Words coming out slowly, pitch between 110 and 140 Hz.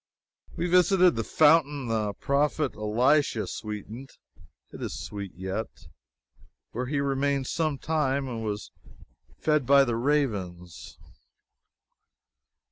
Yes: slow, 110 wpm; low, 135 Hz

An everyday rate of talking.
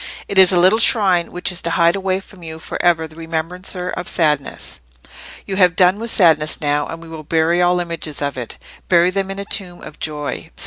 No: fast, 215 wpm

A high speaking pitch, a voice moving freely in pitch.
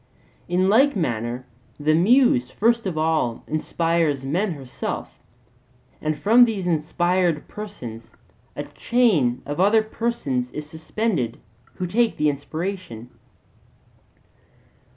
No: medium, 170 Hz; wide, 6.7 semitones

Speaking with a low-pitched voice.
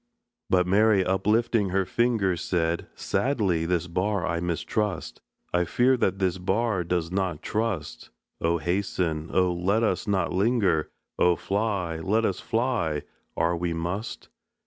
Yes: very low, 95 Hz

